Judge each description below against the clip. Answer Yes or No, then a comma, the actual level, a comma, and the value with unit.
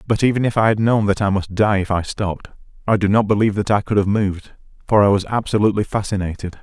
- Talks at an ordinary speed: No, fast, 245 wpm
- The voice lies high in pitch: No, low, 100 Hz